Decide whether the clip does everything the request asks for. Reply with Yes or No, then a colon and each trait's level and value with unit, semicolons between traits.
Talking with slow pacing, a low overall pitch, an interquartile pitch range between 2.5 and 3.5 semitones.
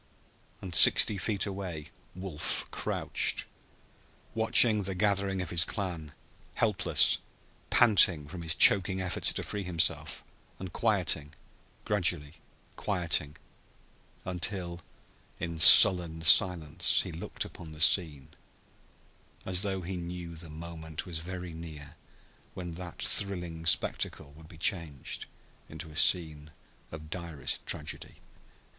Yes: slow, 115 wpm; very low, 85 Hz; average, 2.9 semitones